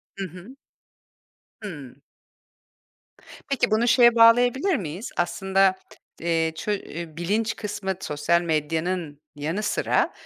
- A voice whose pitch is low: No, medium, 185 Hz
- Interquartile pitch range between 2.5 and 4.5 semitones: No, average, 5.2 semitones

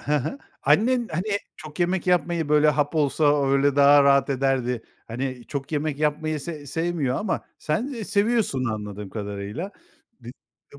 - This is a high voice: No, medium, 150 Hz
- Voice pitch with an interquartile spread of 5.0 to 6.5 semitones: No, average, 4.3 semitones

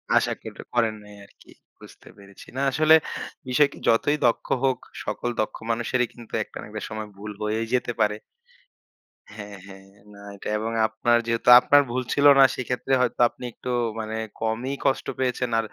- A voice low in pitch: Yes, low, 115 Hz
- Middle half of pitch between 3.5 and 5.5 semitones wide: No, average, 2.8 semitones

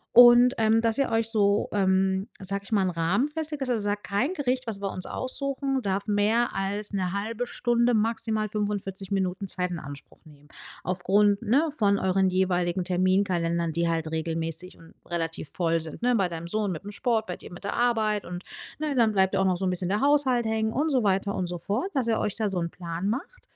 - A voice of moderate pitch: No, high, 200 Hz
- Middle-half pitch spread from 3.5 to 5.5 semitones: Yes, average, 4.0 semitones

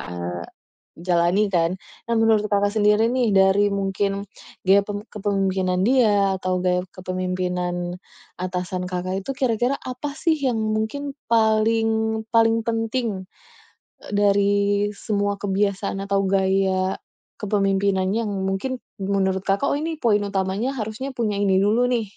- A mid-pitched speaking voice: No, high, 200 Hz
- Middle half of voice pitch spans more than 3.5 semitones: No, average, 2.8 semitones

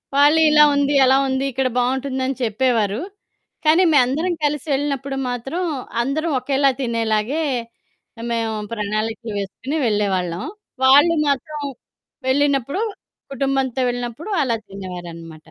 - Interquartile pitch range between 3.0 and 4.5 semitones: Yes, average, 4.1 semitones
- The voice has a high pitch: Yes, very high, 260 Hz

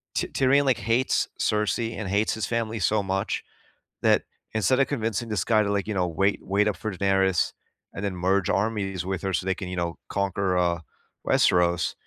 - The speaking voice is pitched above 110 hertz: No, low, 100 Hz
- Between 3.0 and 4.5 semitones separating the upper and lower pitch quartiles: No, narrow, 2.6 semitones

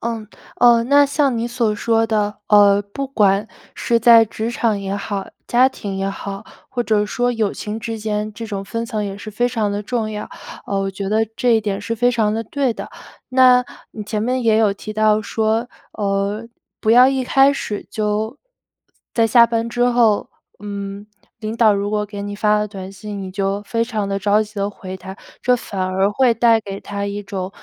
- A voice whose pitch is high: Yes, high, 215 Hz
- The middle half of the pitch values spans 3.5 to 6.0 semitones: No, narrow, 2.4 semitones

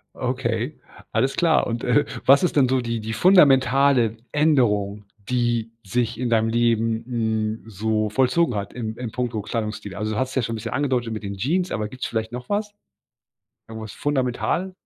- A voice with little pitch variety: No, average, 3.1 semitones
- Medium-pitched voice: No, low, 120 Hz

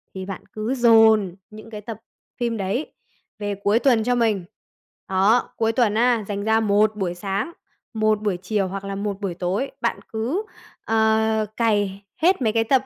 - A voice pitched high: Yes, high, 215 Hz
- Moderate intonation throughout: No, narrow, 2.3 semitones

